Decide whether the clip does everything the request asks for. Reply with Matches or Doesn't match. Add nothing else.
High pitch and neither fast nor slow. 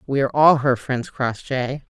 Doesn't match